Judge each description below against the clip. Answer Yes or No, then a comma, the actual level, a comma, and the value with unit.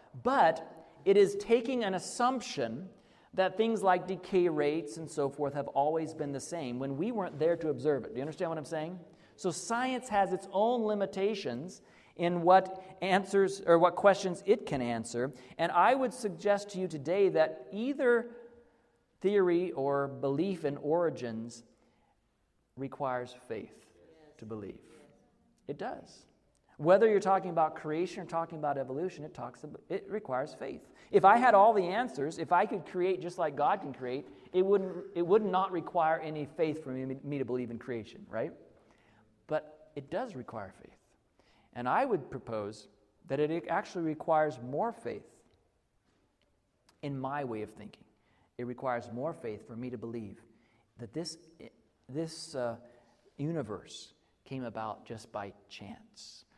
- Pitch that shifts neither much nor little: No, wide, 6.7 semitones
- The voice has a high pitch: No, medium, 160 Hz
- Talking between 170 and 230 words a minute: No, average, 160 wpm